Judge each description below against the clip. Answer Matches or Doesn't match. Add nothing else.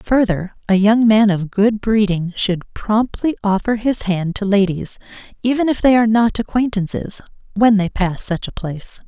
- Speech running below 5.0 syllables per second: Matches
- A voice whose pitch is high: Matches